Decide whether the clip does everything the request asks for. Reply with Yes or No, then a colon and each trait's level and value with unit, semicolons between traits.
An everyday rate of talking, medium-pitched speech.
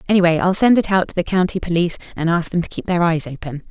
No: fast, 275 wpm; medium, 175 Hz